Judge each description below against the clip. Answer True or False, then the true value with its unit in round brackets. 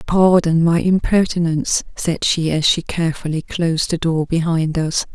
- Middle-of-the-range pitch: True (165 Hz)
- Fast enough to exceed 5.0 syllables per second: False (4.8 syllables/s)